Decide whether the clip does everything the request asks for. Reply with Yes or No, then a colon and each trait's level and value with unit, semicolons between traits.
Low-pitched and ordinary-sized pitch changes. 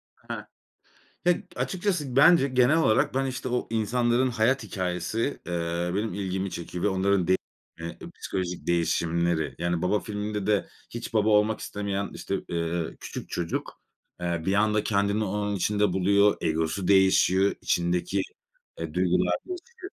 Yes: low, 100 Hz; average, 4.1 semitones